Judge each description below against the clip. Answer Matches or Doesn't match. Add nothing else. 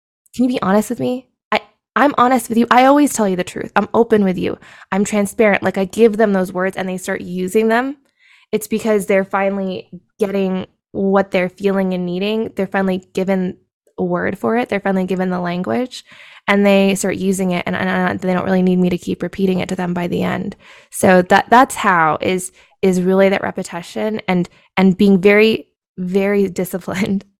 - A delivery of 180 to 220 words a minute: Matches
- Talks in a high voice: Matches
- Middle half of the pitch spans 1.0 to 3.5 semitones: Matches